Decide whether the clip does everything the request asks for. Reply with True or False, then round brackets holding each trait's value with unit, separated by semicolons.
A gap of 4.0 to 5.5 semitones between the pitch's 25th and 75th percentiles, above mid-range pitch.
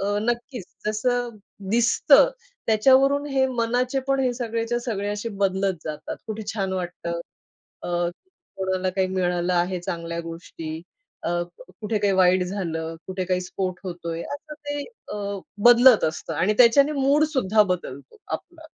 True (5.2 semitones; 205 Hz)